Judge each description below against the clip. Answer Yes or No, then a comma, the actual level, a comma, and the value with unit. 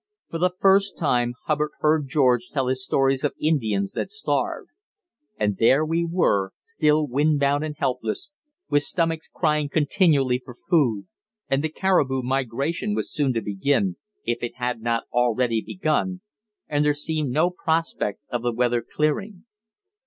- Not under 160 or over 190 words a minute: No, average, 150 wpm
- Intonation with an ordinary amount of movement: Yes, average, 4.6 semitones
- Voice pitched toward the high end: No, medium, 145 Hz